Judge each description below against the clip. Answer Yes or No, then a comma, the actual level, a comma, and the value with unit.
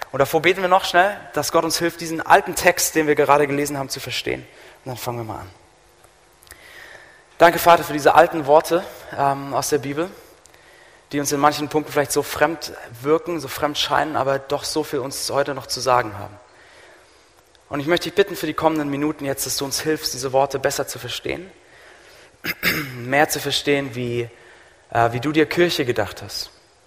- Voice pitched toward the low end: No, medium, 145 Hz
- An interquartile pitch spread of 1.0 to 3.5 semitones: Yes, average, 2.8 semitones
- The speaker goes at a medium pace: No, fast, 195 wpm